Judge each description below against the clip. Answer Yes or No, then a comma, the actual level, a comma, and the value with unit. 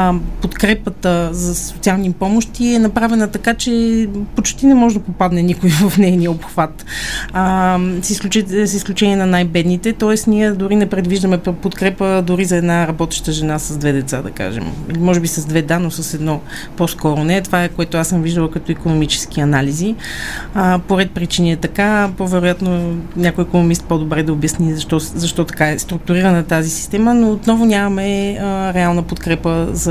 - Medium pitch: Yes, medium, 180 Hz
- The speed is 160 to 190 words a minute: Yes, fast, 165 wpm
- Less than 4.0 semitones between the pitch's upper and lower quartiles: Yes, average, 3.2 semitones